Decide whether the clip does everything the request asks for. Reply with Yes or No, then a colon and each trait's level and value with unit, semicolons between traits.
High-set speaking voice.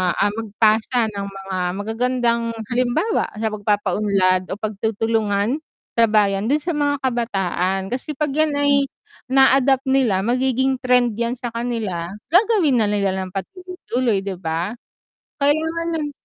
Yes: high, 230 Hz